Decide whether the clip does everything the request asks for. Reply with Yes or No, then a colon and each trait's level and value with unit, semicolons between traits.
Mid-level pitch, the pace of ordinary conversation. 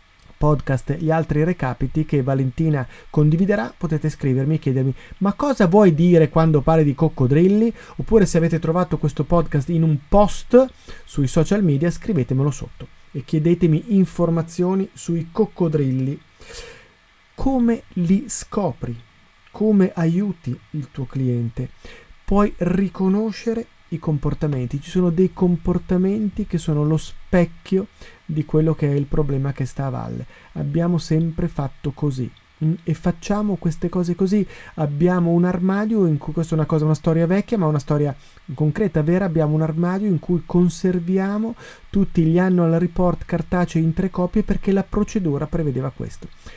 Yes: medium, 165 Hz; average, 145 wpm